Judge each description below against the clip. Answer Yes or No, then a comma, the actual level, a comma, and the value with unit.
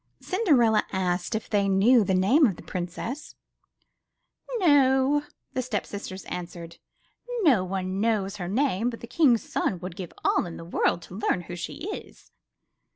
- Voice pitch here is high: Yes, high, 205 Hz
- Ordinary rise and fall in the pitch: No, wide, 5.8 semitones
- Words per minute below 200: Yes, average, 155 wpm